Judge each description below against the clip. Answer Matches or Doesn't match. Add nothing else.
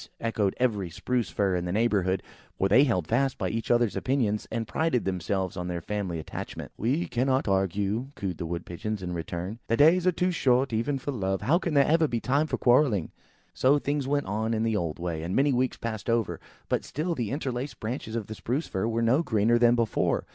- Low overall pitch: Matches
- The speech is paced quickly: Matches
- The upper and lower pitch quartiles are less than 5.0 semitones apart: Doesn't match